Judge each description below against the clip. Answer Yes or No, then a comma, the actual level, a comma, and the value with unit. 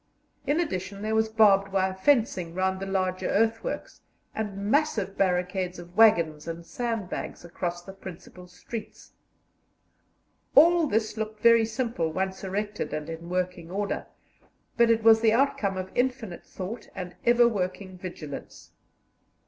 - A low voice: No, high, 195 Hz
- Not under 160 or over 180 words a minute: No, average, 140 wpm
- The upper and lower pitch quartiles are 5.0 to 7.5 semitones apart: No, average, 3.6 semitones